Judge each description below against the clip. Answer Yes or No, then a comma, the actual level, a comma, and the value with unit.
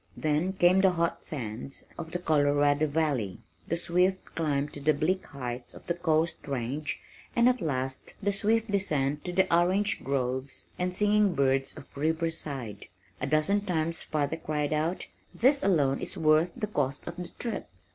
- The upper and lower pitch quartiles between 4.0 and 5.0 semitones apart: Yes, average, 4.5 semitones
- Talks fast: No, average, 165 wpm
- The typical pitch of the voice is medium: Yes, medium, 155 Hz